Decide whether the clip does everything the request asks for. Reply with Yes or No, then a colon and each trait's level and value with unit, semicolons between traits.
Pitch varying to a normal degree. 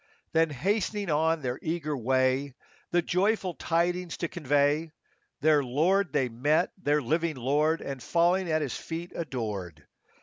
Yes: average, 4.3 semitones